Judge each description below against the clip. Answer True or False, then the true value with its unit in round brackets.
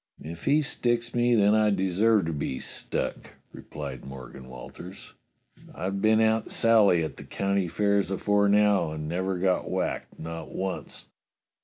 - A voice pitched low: True (95 Hz)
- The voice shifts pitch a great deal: False (4.6 semitones)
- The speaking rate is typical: True (155 wpm)